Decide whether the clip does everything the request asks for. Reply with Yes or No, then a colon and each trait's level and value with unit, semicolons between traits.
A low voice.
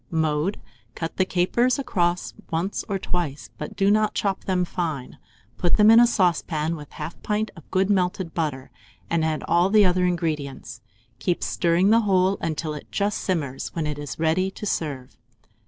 No: medium, 175 Hz